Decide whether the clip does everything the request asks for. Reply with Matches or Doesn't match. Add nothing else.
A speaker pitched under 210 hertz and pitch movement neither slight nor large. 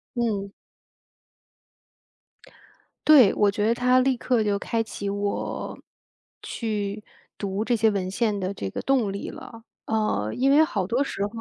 Doesn't match